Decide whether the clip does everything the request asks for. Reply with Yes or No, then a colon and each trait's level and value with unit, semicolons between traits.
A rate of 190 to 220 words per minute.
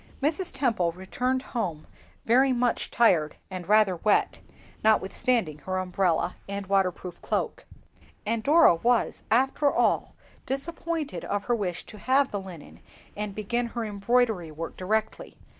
No: average, 140 wpm